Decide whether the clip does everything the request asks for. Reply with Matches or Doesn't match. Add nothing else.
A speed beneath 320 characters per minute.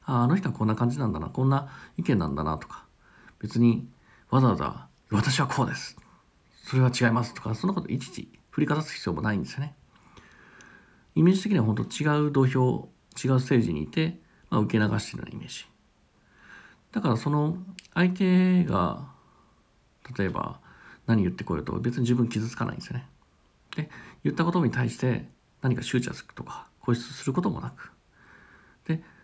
Doesn't match